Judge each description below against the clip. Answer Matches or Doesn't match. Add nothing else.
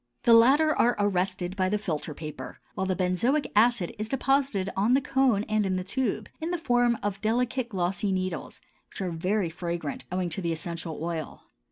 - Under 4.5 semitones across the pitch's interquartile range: Doesn't match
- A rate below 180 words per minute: Doesn't match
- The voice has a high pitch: Matches